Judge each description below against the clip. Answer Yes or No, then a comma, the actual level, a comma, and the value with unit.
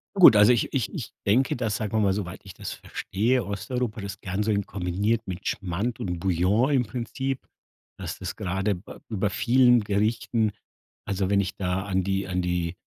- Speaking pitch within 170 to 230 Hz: No, low, 100 Hz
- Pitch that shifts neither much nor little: Yes, average, 3.5 semitones